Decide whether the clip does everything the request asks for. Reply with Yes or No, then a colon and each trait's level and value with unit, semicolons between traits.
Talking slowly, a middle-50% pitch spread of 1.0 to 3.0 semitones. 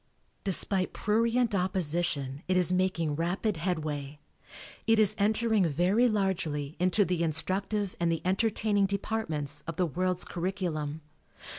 No: slow, 125 wpm; average, 3.9 semitones